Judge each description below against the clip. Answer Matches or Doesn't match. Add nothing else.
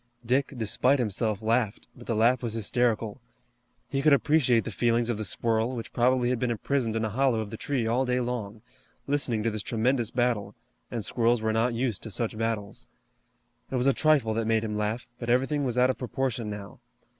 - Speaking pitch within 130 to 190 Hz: Doesn't match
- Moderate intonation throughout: Doesn't match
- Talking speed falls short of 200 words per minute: Doesn't match